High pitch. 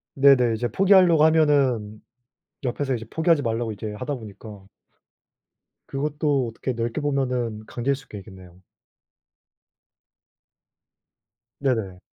No: low, 125 Hz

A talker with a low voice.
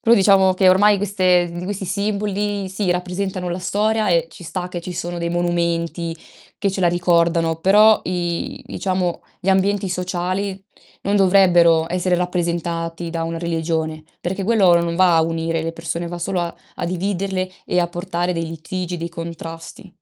No: medium, 180 Hz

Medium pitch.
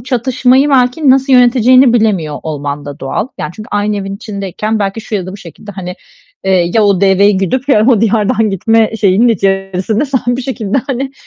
No: high, 215 Hz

